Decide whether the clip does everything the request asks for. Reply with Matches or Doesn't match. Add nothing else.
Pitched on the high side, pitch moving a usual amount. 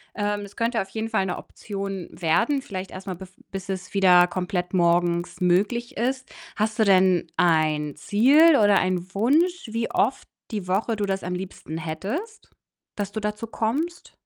Matches